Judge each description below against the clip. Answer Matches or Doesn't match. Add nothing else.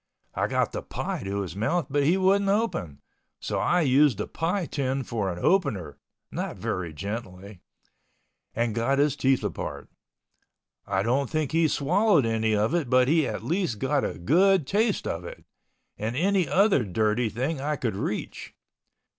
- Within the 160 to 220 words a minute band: Matches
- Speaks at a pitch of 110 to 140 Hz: Matches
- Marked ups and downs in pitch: Matches